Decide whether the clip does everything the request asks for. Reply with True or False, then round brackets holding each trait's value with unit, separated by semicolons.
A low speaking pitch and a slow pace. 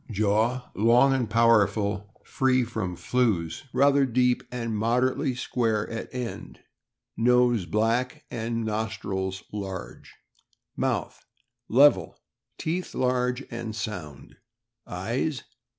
True (115 Hz; 105 wpm)